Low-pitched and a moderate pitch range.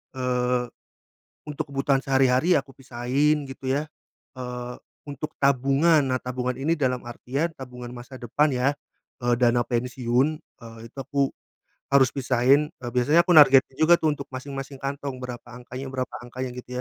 No: low, 130 Hz; narrow, 2.1 semitones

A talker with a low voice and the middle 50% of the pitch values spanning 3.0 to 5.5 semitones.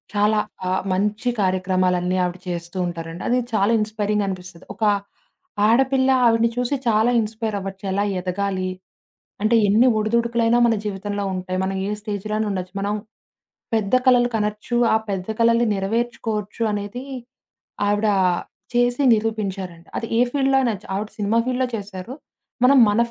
No: high, 210 Hz; average, 3.4 semitones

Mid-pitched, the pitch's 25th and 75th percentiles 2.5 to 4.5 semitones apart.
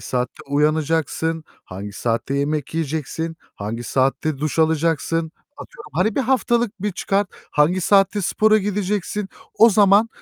No: medium, 165 Hz; wide, 5.6 semitones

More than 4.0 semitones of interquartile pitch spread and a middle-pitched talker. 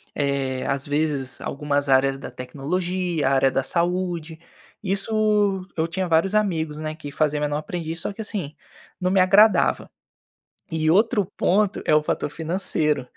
Yes: average, 4.4 semitones; medium, 160 Hz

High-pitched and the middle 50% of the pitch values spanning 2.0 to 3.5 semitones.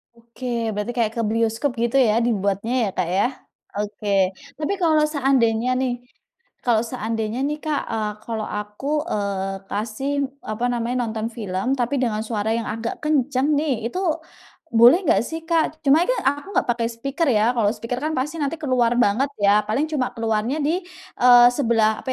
No: high, 235 Hz; average, 4.0 semitones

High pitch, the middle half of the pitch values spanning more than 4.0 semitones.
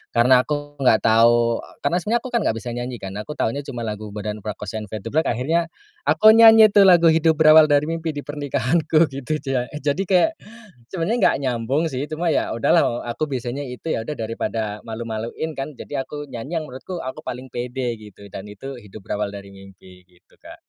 No: low, 130 Hz; wide, 5.6 semitones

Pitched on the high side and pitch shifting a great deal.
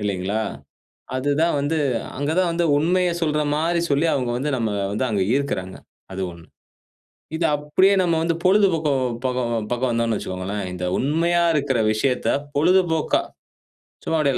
No: medium, 140 Hz; wide, 6.3 semitones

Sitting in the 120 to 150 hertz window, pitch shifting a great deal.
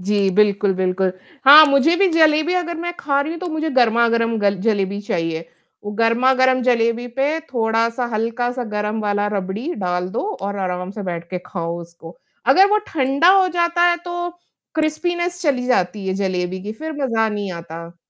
No: high, 230 Hz; wide, 7.7 semitones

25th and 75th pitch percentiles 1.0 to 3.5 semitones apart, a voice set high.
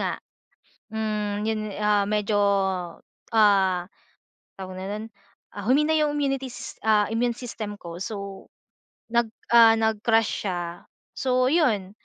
Yes: average, 2.8 semitones; high, 215 Hz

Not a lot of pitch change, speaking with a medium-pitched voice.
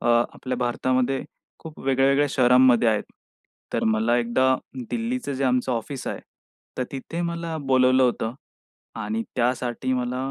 No: narrow, 1.9 semitones; low, 130 Hz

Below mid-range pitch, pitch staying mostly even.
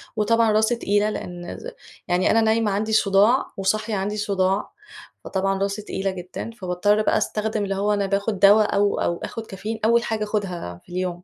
No: high, 205 Hz; narrow, 2.2 semitones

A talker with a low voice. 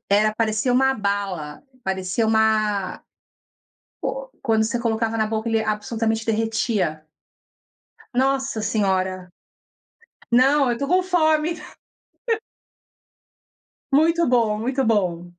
No: high, 220 Hz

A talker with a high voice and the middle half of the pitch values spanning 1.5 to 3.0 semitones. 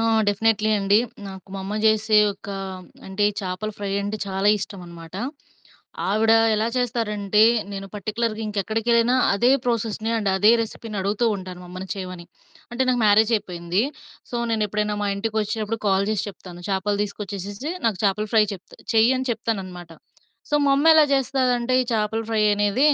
Yes: high, 210 Hz; narrow, 2.5 semitones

